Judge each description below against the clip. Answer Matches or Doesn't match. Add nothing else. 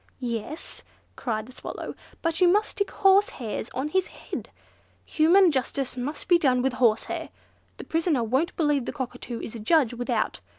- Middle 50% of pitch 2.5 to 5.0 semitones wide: Doesn't match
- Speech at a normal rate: Matches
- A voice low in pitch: Doesn't match